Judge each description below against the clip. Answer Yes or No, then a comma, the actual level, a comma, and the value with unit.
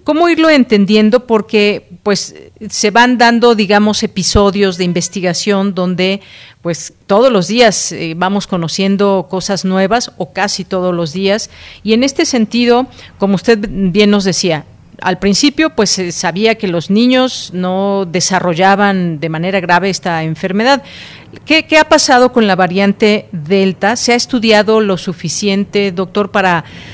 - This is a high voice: Yes, high, 200 Hz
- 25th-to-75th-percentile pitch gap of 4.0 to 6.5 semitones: No, average, 3.3 semitones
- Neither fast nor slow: Yes, average, 145 wpm